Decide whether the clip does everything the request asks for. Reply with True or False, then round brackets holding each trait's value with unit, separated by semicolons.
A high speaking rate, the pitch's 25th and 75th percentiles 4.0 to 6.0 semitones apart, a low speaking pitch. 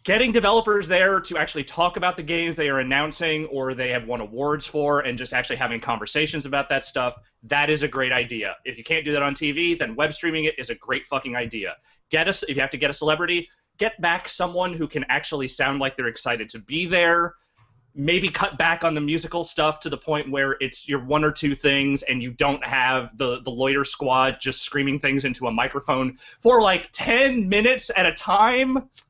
False (220 wpm; 4.3 semitones; 145 Hz)